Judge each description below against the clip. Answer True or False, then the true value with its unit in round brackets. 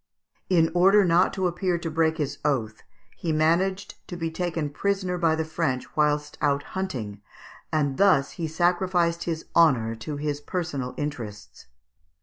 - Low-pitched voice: False (160 Hz)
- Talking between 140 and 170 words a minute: True (150 wpm)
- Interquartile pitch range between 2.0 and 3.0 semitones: False (3.4 semitones)